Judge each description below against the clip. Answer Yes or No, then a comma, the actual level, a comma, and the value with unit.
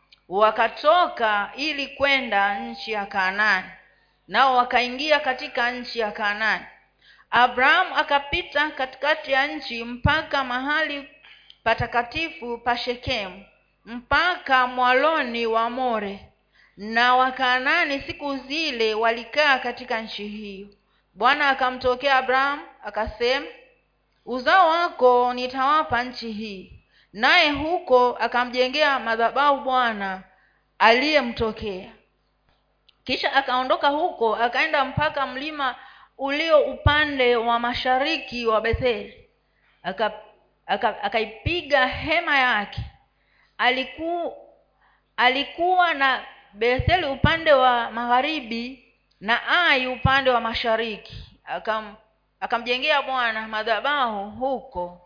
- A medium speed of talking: No, slow, 90 wpm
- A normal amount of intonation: Yes, average, 3.8 semitones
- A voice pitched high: Yes, very high, 250 Hz